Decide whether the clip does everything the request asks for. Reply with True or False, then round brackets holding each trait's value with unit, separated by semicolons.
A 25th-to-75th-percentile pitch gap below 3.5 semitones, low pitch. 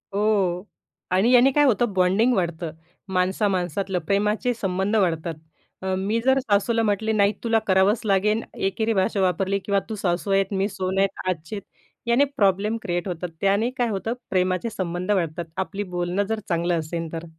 False (2.9 semitones; 195 Hz)